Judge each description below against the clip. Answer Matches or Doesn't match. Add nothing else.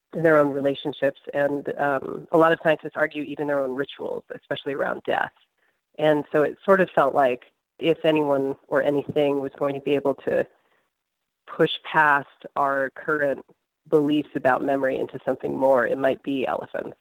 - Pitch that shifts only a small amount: Matches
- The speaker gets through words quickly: Doesn't match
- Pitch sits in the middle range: Matches